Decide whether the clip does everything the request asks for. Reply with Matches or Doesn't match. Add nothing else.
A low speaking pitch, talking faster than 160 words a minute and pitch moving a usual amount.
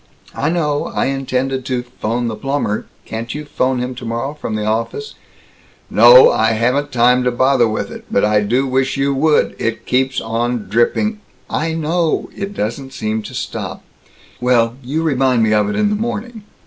Matches